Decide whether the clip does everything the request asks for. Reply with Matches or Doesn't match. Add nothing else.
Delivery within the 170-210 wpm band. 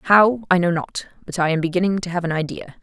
Doesn't match